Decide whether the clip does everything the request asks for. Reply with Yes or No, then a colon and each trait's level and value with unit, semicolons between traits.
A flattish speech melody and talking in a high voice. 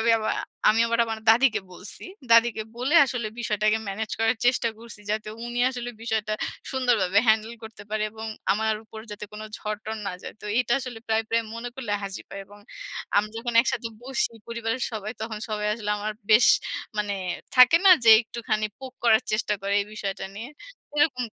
Yes: narrow, 1.9 semitones; high, 220 Hz